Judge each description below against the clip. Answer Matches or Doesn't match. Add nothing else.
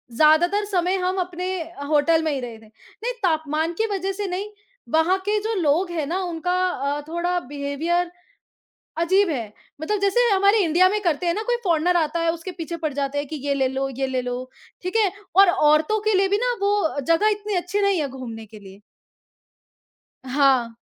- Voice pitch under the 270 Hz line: Doesn't match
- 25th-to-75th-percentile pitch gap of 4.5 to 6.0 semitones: Matches